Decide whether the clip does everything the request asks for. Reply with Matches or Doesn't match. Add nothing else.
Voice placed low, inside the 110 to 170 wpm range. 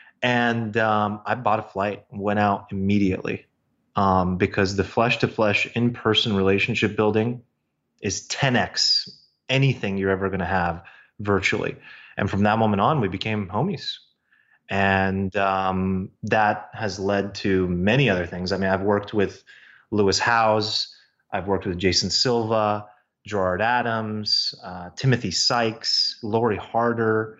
Matches